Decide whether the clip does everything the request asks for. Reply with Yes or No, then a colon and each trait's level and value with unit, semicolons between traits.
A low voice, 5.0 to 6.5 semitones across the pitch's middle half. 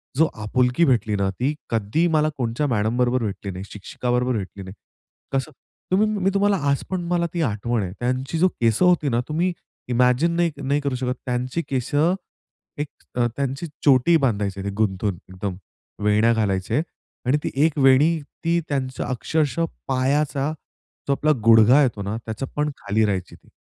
Yes: low, 125 Hz; average, 5.3 semitones